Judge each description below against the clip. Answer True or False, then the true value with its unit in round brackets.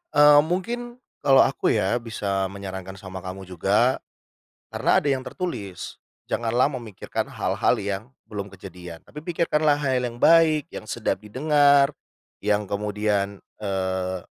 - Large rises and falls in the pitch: True (7.1 semitones)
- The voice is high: False (110 Hz)